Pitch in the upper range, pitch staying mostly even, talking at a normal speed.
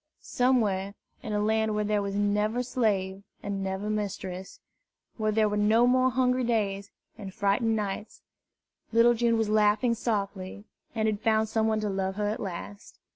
Yes: high, 210 Hz; narrow, 2.0 semitones; average, 170 wpm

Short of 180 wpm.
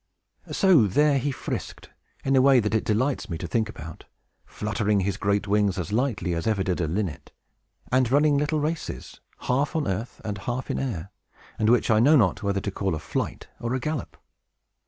No: average, 200 wpm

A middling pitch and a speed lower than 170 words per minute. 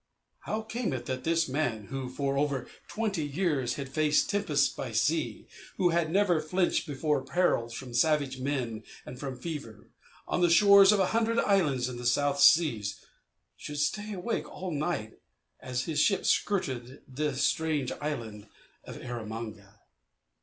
Yes: medium, 145 Hz; average, 155 wpm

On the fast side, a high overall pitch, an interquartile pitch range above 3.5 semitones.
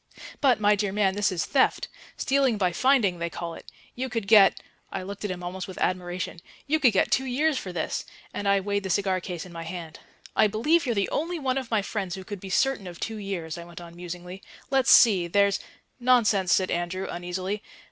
Yes: fast, 225 wpm; high, 195 Hz; average, 4.3 semitones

